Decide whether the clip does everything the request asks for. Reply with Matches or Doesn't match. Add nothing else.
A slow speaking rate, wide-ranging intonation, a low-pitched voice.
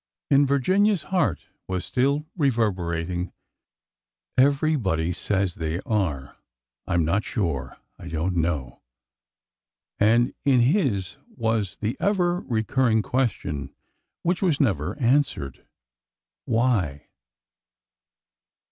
Matches